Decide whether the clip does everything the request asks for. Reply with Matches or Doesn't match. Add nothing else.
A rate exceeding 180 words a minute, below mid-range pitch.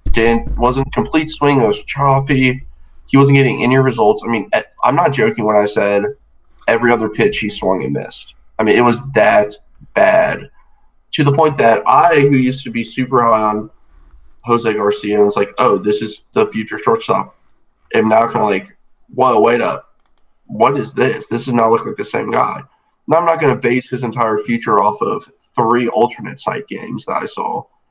Matches